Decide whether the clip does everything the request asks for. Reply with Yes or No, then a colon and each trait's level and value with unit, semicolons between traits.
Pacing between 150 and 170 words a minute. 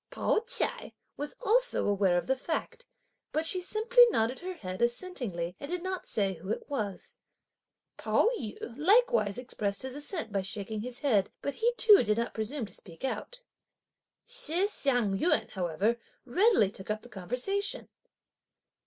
Yes: average, 160 wpm